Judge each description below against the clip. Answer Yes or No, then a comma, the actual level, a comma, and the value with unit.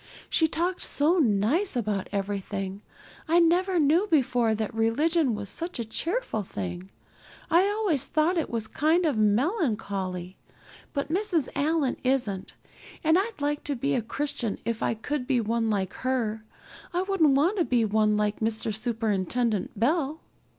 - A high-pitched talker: Yes, very high, 250 Hz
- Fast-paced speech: No, average, 155 wpm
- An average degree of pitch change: No, wide, 7.2 semitones